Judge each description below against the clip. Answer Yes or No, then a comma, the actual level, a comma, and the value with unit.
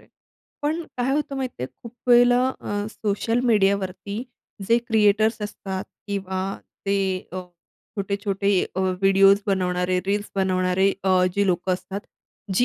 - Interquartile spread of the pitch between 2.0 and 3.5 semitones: Yes, average, 2.8 semitones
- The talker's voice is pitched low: No, high, 200 Hz